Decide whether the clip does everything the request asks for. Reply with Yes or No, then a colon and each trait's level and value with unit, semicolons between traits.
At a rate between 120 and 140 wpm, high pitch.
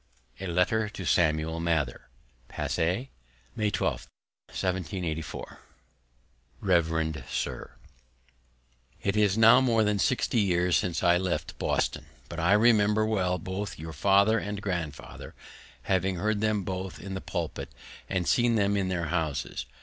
No: slow, 135 wpm; very low, 95 Hz